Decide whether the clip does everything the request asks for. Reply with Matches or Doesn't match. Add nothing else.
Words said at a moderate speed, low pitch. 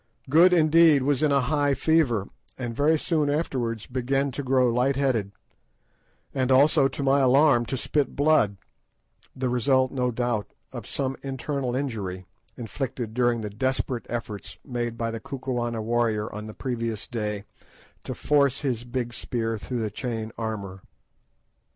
Matches